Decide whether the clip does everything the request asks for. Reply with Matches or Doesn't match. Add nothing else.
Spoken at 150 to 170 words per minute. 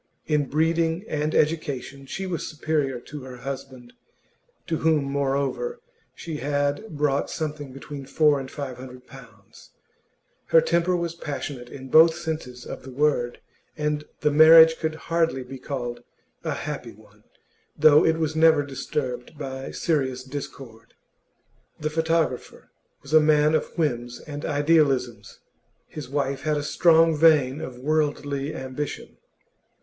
Doesn't match